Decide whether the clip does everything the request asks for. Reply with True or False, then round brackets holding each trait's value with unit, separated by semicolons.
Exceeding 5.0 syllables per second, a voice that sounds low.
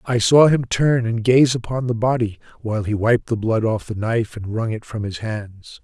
False (4.9 syllables/s; 115 Hz)